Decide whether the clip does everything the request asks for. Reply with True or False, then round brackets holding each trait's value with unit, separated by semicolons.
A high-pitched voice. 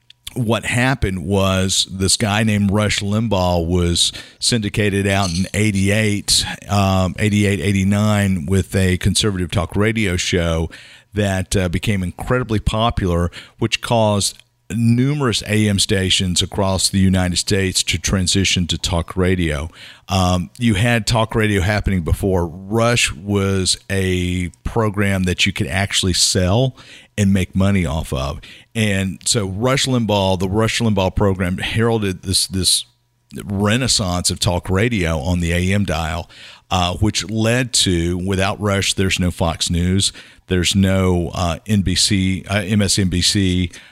False (95 Hz)